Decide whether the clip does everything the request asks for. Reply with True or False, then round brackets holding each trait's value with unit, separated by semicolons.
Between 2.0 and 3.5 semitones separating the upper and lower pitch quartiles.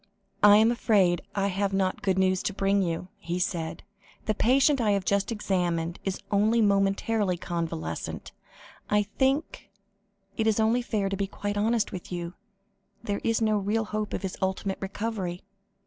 True (2.7 semitones)